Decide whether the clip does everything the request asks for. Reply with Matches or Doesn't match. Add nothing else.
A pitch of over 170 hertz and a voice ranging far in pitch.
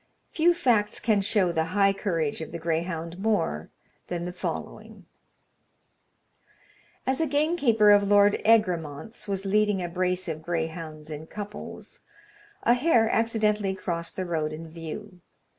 Doesn't match